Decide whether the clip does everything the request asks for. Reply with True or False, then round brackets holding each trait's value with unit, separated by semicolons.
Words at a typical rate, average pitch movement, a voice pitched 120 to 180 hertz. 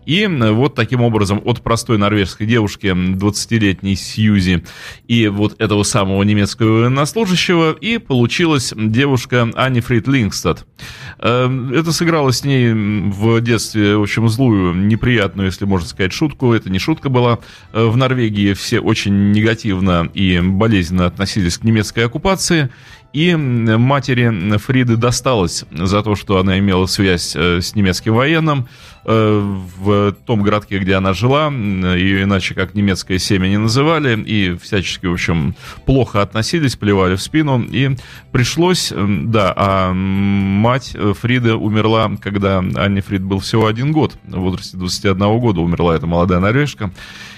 False (135 wpm; 4.0 semitones; 110 Hz)